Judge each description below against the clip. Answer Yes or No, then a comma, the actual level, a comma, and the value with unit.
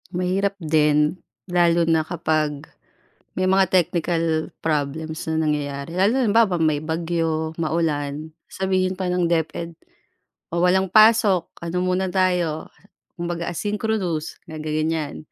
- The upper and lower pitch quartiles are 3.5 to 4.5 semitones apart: No, average, 2.7 semitones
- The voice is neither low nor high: Yes, medium, 170 Hz